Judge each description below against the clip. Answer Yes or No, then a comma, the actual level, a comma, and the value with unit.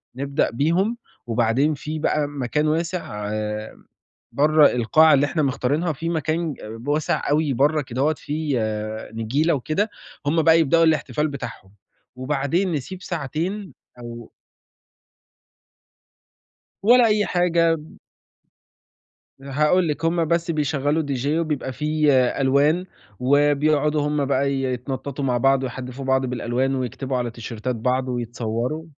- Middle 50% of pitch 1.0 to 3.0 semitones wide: No, average, 3.6 semitones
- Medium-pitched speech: Yes, medium, 145 Hz